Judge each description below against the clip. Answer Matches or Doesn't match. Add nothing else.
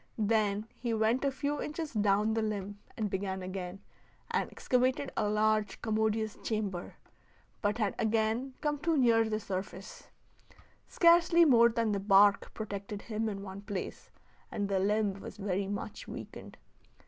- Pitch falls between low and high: Doesn't match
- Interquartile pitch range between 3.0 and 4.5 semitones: Doesn't match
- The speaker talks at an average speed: Matches